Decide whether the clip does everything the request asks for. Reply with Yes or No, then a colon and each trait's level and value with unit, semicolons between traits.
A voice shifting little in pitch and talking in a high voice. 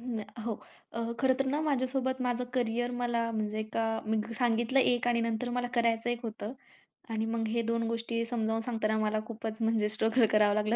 Yes: narrow, 1.7 semitones; high, 230 Hz